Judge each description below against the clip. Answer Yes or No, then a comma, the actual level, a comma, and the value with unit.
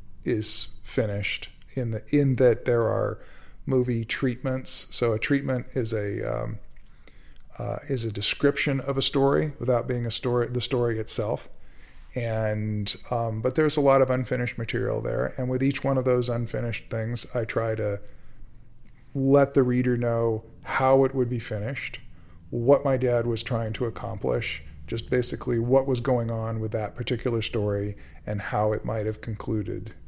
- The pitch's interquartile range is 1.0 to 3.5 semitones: Yes, narrow, 2.6 semitones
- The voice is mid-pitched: No, low, 120 Hz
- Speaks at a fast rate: No, average, 165 wpm